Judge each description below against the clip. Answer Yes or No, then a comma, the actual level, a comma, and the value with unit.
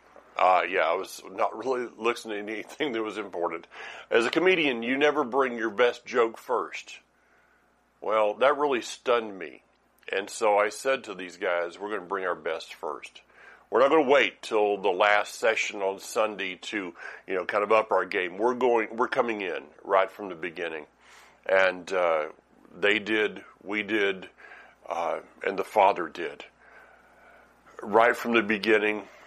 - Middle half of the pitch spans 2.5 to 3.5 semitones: Yes, average, 2.9 semitones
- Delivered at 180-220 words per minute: No, average, 170 wpm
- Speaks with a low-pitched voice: Yes, low, 110 Hz